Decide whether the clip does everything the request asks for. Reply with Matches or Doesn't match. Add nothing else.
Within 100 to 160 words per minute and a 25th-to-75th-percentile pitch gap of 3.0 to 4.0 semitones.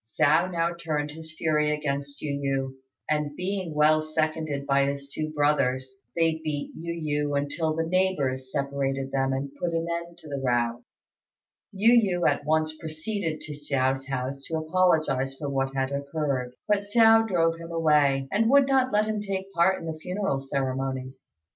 Doesn't match